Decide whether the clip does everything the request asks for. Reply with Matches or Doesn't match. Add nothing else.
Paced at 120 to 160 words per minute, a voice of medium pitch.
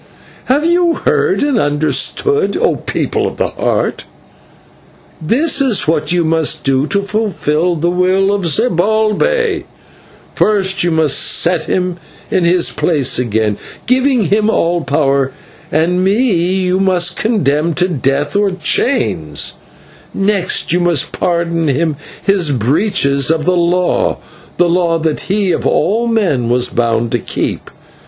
Matches